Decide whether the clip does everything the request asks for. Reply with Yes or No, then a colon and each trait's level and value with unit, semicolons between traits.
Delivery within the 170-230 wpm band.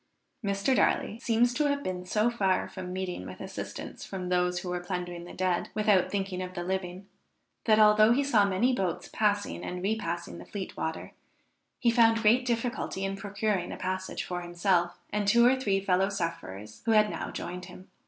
Yes: average, 190 wpm